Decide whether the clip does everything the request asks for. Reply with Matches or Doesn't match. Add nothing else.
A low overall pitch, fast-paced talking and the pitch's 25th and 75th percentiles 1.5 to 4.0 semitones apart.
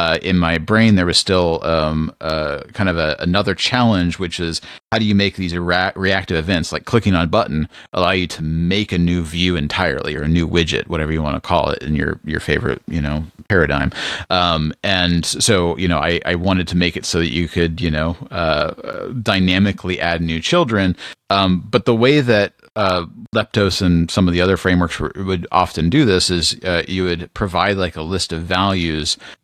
Matches